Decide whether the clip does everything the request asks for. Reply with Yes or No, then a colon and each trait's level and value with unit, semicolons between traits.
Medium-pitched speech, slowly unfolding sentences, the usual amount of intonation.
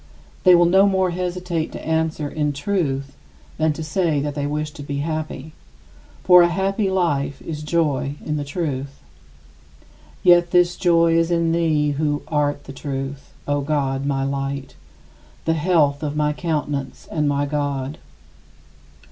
No: medium, 150 Hz; average, 155 wpm; average, 3.1 semitones